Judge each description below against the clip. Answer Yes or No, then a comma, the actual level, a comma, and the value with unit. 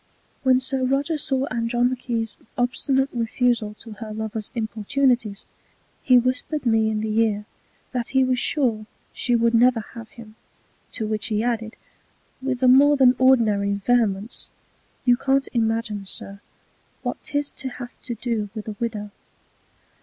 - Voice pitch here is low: No, high, 235 Hz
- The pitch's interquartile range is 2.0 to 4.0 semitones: Yes, average, 2.9 semitones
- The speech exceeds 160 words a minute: No, average, 145 wpm